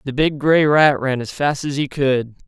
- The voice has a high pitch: No, medium, 140 Hz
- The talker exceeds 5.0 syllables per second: No, 4.5 syllables/s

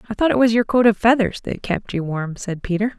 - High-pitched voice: Yes, high, 215 Hz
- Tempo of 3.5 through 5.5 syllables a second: No, 5.8 syllables/s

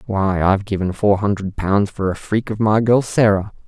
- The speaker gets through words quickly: Yes, fast, 210 wpm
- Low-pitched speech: Yes, low, 100 Hz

